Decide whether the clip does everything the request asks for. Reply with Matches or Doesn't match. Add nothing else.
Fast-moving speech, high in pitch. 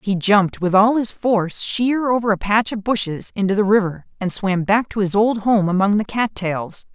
Matches